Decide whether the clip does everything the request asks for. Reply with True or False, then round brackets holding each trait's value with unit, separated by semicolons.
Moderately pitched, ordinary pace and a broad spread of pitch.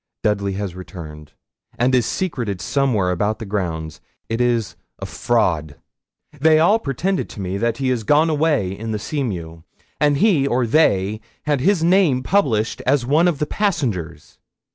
False (120 Hz; 165 wpm; 7.2 semitones)